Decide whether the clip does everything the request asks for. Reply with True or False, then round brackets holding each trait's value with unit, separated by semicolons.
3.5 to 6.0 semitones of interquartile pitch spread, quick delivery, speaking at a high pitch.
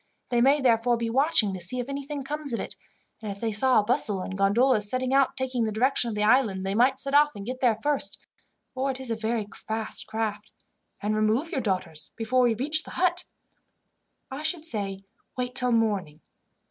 True (4.1 semitones; 210 wpm; 235 Hz)